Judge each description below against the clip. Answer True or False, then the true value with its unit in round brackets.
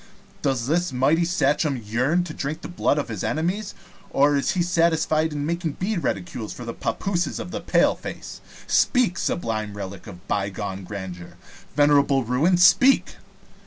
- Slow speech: False (155 wpm)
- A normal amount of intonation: False (7.0 semitones)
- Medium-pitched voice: True (145 Hz)